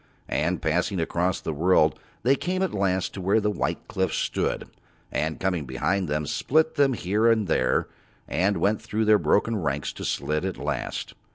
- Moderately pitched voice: No, very low, 95 Hz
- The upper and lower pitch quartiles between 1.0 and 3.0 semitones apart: No, average, 5.1 semitones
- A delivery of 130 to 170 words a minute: No, average, 180 wpm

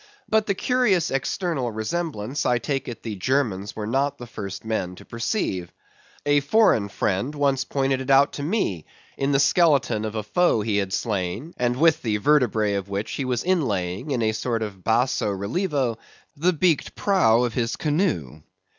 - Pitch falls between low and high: No, low, 125 Hz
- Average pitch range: No, wide, 5.7 semitones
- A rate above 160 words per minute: Yes, average, 180 wpm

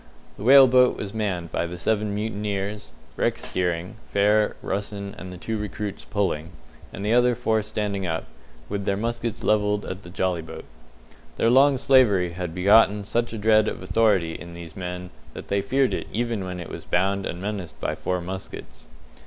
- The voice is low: Yes, low, 100 Hz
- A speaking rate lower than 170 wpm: No, average, 185 wpm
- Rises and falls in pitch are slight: No, average, 3.3 semitones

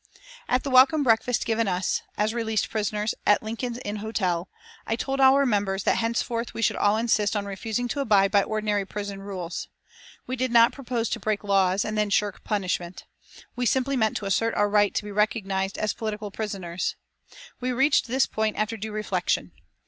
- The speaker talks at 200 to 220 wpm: No, average, 185 wpm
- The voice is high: Yes, high, 215 Hz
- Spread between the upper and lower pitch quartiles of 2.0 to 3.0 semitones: Yes, narrow, 2.5 semitones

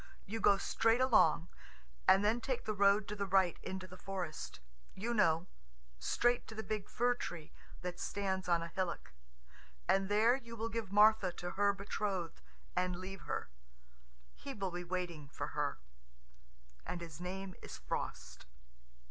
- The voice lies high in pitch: Yes, high, 195 Hz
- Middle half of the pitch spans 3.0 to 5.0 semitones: Yes, average, 3.3 semitones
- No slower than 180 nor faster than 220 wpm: No, average, 160 wpm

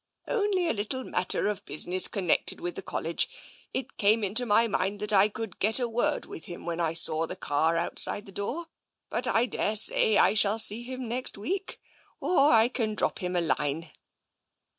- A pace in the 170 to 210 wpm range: Yes, average, 200 wpm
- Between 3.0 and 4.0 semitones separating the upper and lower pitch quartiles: No, average, 5.0 semitones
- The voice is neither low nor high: No, high, 210 Hz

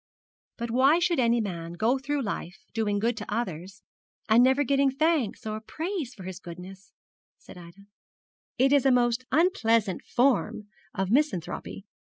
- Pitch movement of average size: No, wide, 5.8 semitones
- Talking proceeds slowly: No, average, 155 wpm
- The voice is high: Yes, high, 230 Hz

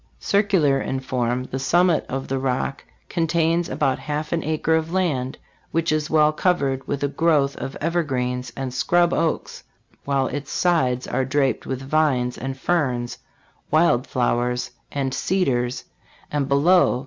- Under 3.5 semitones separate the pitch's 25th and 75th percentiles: No, average, 3.9 semitones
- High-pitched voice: No, medium, 140 Hz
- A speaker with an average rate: Yes, average, 150 wpm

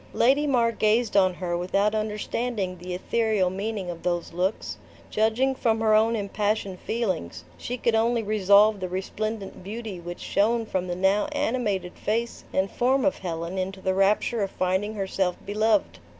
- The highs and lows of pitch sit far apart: No, average, 3.2 semitones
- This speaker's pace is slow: No, average, 165 wpm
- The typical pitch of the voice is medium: No, high, 205 Hz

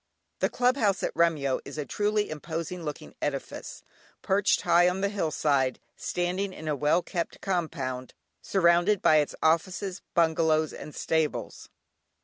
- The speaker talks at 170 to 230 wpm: No, average, 145 wpm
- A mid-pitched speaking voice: Yes, medium, 170 Hz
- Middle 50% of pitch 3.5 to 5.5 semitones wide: Yes, average, 3.8 semitones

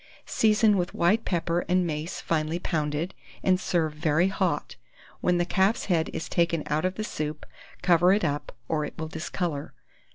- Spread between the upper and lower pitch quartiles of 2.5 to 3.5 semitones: Yes, average, 2.9 semitones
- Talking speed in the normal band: Yes, average, 170 wpm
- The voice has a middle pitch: Yes, medium, 170 Hz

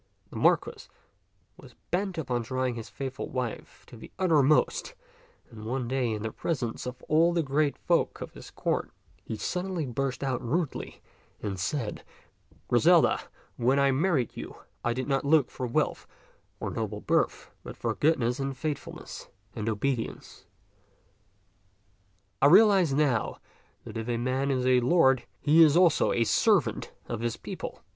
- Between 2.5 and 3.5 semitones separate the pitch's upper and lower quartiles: No, average, 4.3 semitones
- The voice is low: Yes, low, 130 Hz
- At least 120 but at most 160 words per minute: Yes, average, 155 wpm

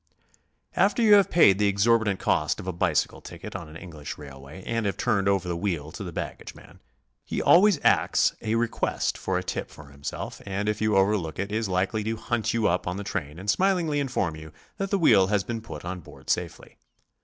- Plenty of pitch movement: No, average, 4.7 semitones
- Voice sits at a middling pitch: No, low, 100 Hz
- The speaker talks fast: Yes, fast, 215 wpm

